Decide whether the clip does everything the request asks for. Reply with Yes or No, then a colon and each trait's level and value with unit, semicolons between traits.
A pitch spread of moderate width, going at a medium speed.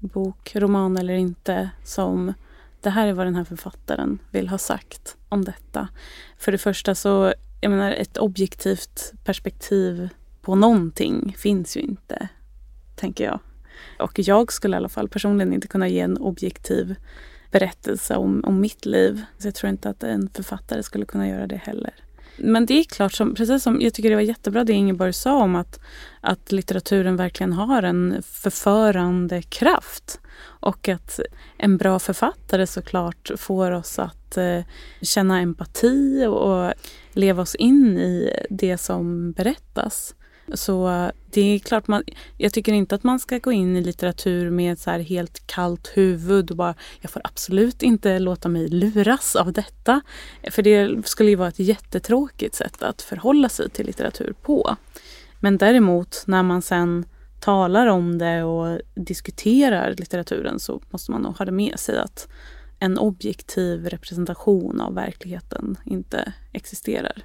Yes: average, 3.2 semitones; average, 160 wpm